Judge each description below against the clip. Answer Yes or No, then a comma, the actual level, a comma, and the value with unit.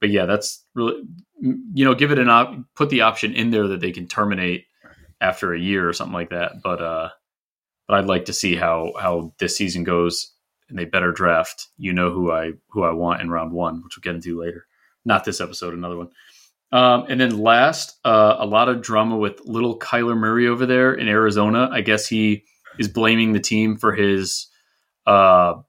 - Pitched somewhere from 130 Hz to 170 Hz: No, low, 105 Hz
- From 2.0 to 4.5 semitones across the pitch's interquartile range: No, average, 5.0 semitones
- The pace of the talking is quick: Yes, fast, 210 wpm